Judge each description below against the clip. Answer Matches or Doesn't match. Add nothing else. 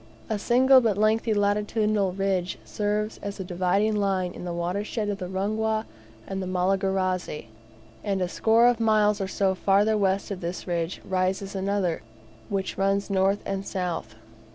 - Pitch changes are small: Matches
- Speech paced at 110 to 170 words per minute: Matches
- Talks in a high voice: Matches